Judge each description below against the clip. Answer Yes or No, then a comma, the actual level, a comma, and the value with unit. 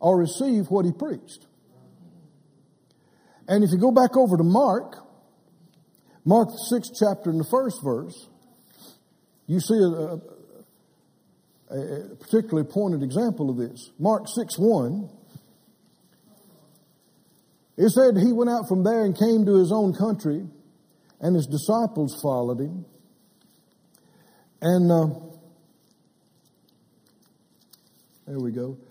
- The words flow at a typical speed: No, slow, 115 wpm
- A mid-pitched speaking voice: Yes, medium, 180 Hz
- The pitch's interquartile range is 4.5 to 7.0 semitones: Yes, wide, 5.6 semitones